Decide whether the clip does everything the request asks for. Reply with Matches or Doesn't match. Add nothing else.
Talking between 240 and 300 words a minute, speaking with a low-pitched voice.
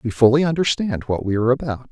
Doesn't match